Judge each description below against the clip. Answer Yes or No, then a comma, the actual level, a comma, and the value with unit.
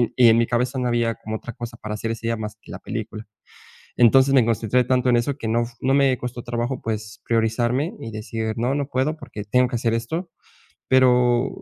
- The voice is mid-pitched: No, low, 120 Hz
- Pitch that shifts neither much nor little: No, narrow, 2.1 semitones